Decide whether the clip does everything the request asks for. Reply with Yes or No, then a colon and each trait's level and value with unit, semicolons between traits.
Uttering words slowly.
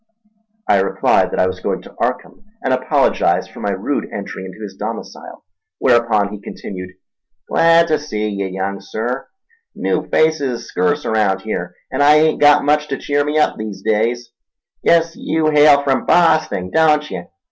No: average, 170 wpm